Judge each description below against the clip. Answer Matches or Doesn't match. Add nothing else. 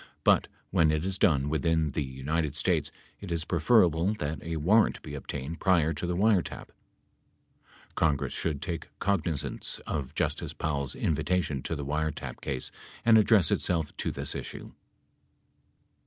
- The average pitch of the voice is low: Matches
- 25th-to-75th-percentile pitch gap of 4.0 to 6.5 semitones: Doesn't match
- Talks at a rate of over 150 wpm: Doesn't match